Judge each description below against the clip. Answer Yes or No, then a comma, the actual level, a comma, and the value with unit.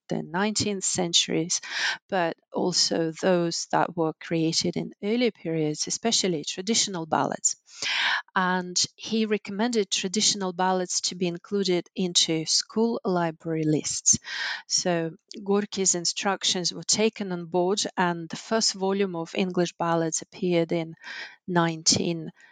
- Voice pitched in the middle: Yes, medium, 180 Hz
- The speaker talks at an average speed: No, slow, 120 wpm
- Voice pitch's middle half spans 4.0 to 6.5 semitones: No, average, 3.3 semitones